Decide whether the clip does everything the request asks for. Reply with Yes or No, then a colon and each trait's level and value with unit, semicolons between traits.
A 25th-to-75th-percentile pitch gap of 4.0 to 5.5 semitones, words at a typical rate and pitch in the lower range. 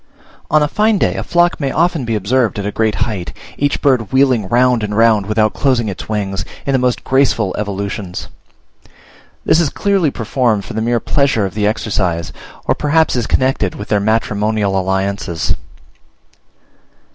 Yes: average, 4.8 semitones; average, 170 wpm; low, 110 Hz